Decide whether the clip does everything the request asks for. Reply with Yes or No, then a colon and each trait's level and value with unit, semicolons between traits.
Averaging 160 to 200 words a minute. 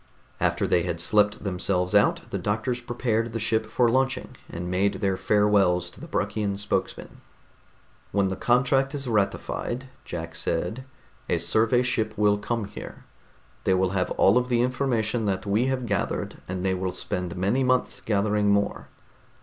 Yes: average, 165 wpm